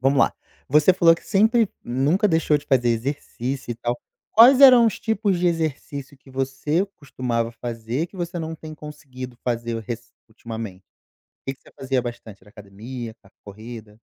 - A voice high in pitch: No, low, 135 Hz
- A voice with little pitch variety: No, wide, 5.6 semitones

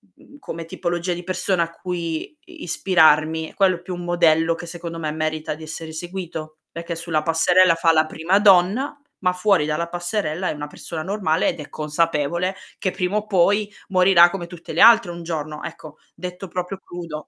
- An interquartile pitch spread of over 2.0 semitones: Yes, narrow, 2.4 semitones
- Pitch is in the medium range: Yes, medium, 170 Hz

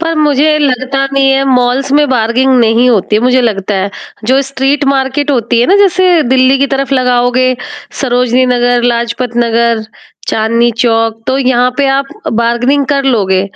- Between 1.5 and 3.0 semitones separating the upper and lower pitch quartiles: Yes, narrow, 2.6 semitones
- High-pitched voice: Yes, very high, 250 Hz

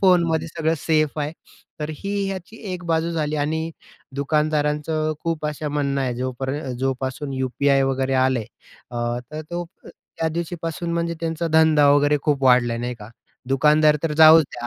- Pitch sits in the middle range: Yes, medium, 150 Hz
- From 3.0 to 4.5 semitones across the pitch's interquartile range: Yes, average, 3.3 semitones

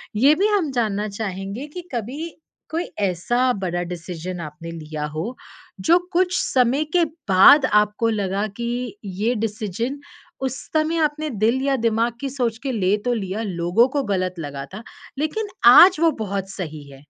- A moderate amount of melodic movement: No, wide, 7.0 semitones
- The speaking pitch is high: Yes, high, 220 Hz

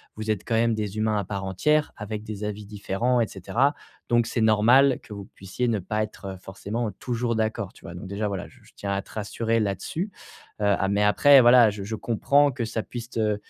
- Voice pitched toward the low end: Yes, low, 110 Hz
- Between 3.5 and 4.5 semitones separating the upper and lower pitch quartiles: No, average, 2.8 semitones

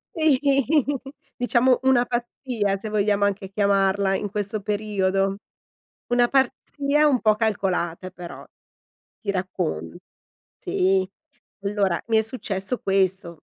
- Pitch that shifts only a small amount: No, average, 3.7 semitones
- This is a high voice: Yes, high, 200 Hz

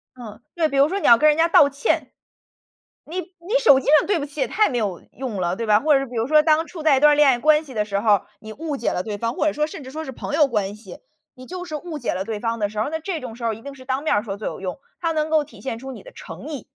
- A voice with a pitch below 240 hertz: No, very high, 270 Hz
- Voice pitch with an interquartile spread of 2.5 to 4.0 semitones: No, wide, 5.6 semitones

